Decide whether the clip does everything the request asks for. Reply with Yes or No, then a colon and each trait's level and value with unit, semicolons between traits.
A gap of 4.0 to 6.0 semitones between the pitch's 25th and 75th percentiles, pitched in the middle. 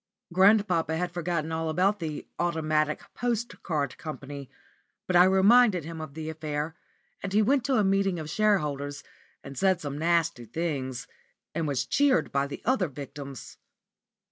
Yes: average, 4.5 semitones; medium, 165 Hz